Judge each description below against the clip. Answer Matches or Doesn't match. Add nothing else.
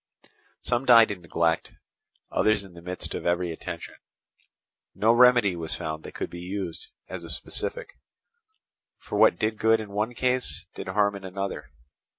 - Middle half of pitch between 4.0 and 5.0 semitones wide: Matches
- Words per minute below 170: Matches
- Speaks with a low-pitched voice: Matches